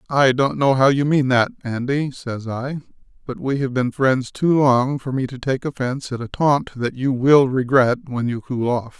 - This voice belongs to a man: Yes, male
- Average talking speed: No, fast, 220 wpm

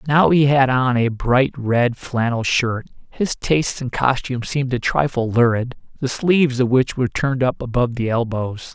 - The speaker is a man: Yes, male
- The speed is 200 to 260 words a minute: No, average, 170 wpm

